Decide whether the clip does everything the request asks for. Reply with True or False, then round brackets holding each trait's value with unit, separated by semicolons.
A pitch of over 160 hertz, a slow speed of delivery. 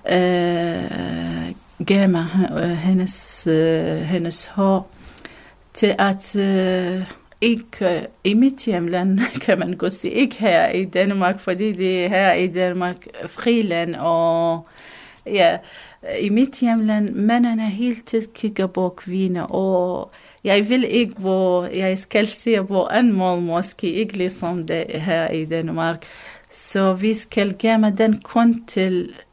True (190 Hz; 130 wpm)